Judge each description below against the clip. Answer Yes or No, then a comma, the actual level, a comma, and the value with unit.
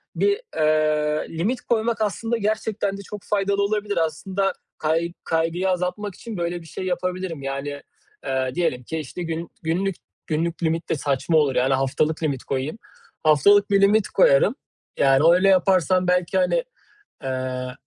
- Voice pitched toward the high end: No, medium, 170 Hz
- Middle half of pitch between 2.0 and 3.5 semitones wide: No, average, 4.6 semitones